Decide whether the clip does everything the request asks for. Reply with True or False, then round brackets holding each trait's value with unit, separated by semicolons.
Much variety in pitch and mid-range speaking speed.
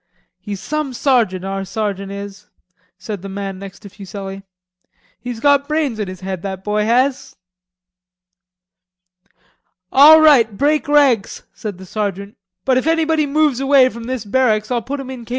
True (5.7 semitones; 160 wpm)